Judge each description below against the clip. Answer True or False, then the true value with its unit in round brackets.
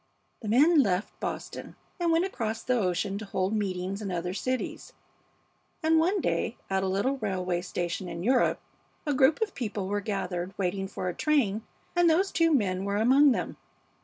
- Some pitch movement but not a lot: False (6.7 semitones)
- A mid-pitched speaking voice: False (210 Hz)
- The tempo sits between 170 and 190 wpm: True (180 wpm)